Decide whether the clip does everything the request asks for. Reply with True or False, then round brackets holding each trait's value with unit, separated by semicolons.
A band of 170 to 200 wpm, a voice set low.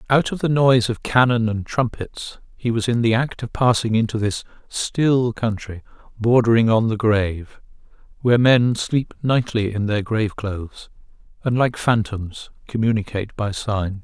False (160 wpm; 115 Hz)